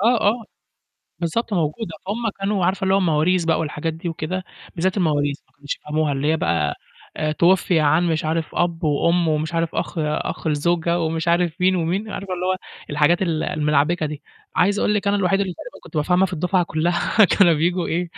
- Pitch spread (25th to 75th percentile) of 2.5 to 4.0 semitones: Yes, average, 3.0 semitones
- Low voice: No, medium, 170 Hz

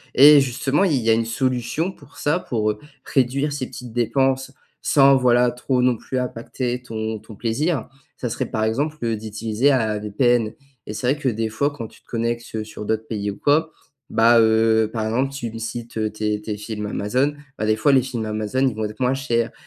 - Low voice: Yes, low, 120 Hz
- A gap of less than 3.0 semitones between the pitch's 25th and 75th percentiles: No, average, 3.3 semitones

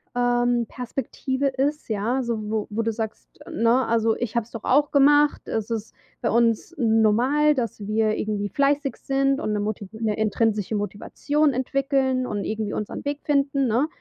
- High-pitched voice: Yes, high, 235 Hz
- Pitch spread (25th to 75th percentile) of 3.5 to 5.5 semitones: Yes, average, 3.9 semitones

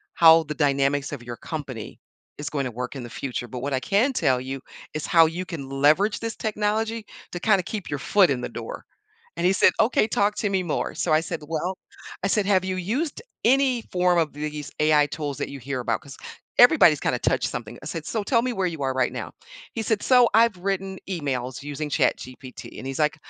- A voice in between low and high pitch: Yes, medium, 165 Hz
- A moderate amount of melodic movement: No, wide, 6.5 semitones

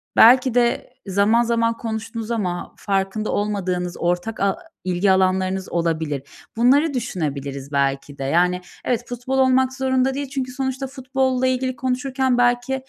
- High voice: Yes, high, 230 Hz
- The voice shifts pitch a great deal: Yes, wide, 6.0 semitones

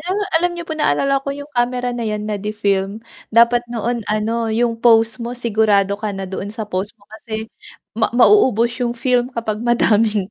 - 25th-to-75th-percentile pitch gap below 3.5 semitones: Yes, narrow, 2.4 semitones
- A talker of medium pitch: No, high, 230 Hz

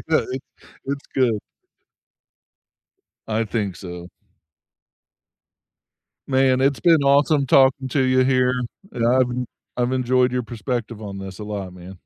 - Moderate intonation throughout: Yes, average, 3.7 semitones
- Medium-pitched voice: No, low, 125 Hz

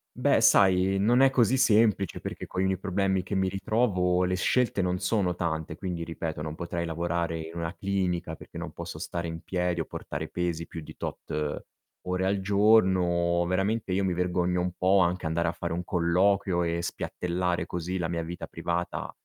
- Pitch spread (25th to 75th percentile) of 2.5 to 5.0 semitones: No, narrow, 2.1 semitones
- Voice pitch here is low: Yes, very low, 90 Hz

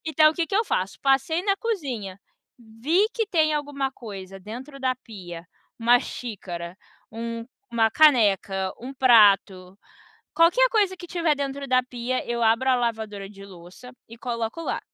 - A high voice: Yes, high, 245 Hz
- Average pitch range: No, wide, 6.3 semitones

